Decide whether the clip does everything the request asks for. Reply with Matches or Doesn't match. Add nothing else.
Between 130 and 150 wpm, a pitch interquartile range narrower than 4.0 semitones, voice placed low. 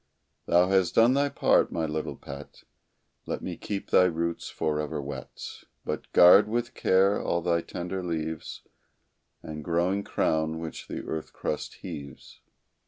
Matches